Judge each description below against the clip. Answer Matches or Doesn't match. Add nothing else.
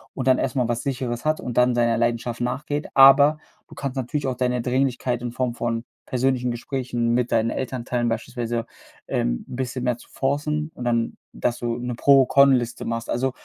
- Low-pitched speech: Matches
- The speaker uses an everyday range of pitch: Doesn't match